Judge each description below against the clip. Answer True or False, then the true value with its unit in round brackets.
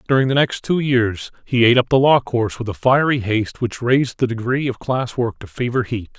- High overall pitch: False (120 Hz)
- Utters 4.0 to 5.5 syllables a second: False (5.7 syllables/s)